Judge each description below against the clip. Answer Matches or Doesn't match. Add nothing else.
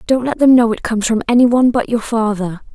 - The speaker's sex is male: Doesn't match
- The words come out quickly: Matches